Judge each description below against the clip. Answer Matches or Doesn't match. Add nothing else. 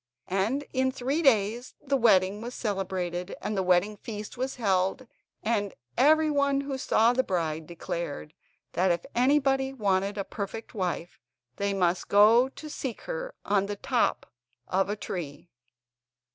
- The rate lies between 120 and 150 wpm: Matches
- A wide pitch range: Matches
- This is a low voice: Doesn't match